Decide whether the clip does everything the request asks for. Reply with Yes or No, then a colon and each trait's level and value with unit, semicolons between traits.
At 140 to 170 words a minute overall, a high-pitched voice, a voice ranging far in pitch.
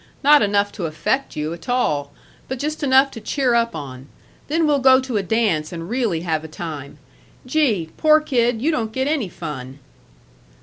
No: average, 185 wpm; high, 225 Hz; wide, 8.6 semitones